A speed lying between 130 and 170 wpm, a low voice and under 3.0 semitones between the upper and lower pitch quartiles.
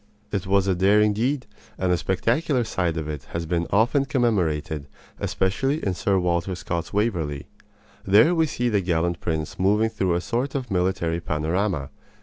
No: average, 165 wpm; very low, 95 Hz; average, 4.8 semitones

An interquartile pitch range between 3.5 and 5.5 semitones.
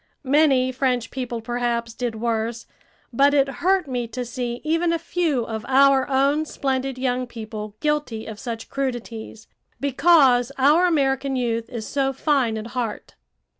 No: average, 3.0 semitones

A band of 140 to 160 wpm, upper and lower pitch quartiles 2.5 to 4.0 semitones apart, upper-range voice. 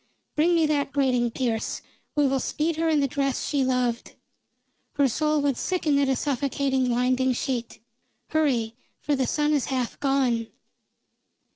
Yes: average, 155 wpm; average, 2.8 semitones; very high, 275 Hz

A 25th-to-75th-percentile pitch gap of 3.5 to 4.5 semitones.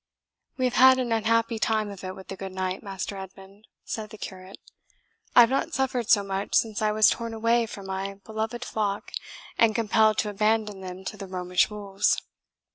No: average, 2.8 semitones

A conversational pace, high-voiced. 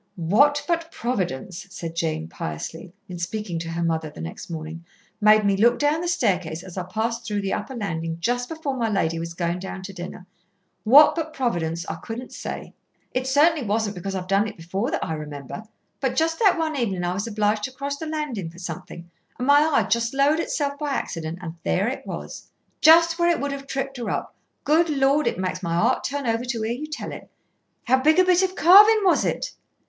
No: fast, 215 wpm; high, 225 Hz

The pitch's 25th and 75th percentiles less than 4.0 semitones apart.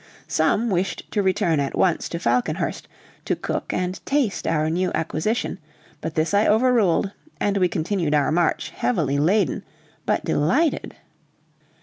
No: average, 4.6 semitones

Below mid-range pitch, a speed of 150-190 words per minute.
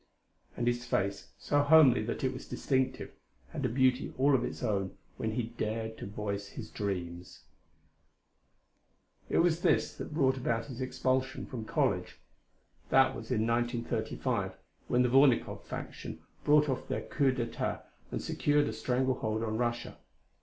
Yes: low, 120 Hz; average, 155 wpm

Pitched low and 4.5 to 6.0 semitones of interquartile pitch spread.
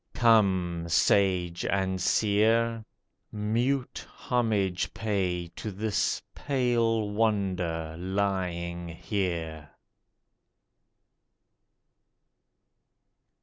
No: low, 100 Hz; average, 4.1 semitones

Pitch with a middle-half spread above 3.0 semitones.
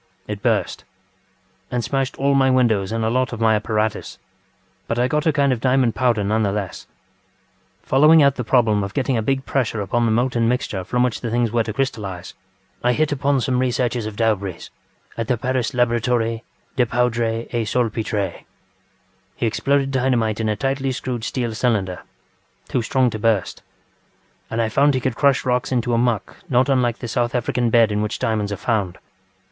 No: average, 2.7 semitones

